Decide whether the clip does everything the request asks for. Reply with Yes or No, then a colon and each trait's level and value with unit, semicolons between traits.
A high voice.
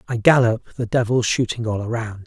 No: low, 115 Hz